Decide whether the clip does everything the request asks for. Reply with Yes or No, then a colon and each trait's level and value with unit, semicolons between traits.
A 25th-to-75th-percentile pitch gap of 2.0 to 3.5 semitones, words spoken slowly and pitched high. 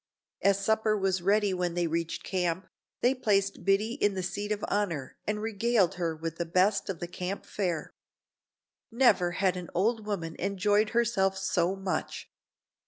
No: average, 2.9 semitones; average, 165 wpm; high, 195 Hz